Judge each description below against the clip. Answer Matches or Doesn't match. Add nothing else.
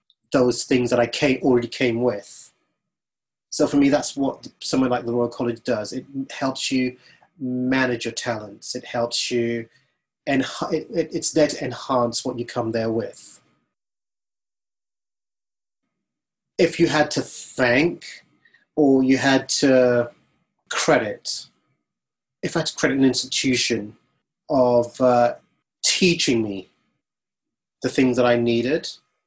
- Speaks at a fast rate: Doesn't match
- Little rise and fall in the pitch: Matches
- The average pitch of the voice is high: Doesn't match